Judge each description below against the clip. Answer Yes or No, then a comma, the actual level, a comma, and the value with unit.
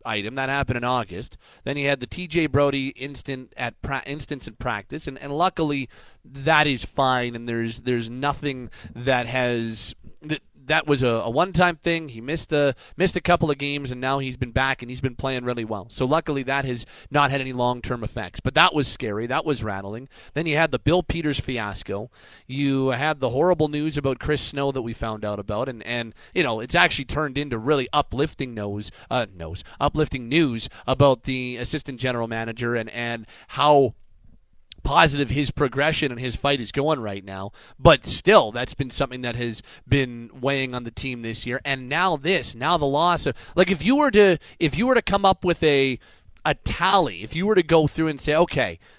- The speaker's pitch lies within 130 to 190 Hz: Yes, low, 135 Hz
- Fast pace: Yes, fast, 210 wpm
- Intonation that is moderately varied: Yes, average, 3.9 semitones